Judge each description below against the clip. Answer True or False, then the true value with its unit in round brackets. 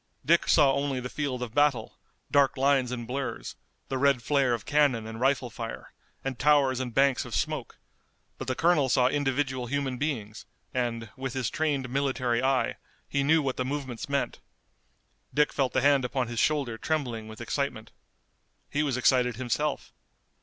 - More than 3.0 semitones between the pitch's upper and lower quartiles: False (2.4 semitones)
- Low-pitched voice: True (130 Hz)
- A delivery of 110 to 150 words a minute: False (170 wpm)